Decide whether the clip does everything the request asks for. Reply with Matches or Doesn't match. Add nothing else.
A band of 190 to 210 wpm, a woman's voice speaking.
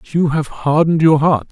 Doesn't match